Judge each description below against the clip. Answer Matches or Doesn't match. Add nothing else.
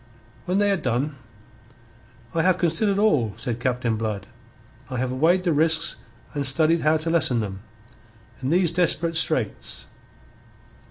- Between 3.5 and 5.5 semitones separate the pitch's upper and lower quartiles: Matches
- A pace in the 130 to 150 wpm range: Matches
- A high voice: Doesn't match